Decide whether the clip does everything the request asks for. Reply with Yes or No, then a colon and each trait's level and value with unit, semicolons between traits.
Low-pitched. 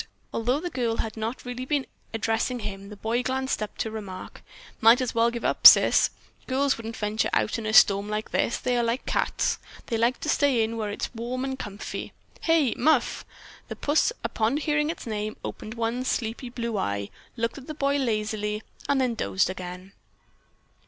No: high, 230 Hz